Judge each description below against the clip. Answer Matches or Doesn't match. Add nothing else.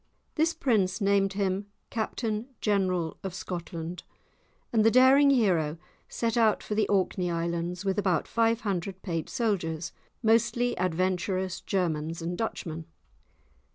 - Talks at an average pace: Doesn't match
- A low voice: Doesn't match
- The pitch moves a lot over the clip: Doesn't match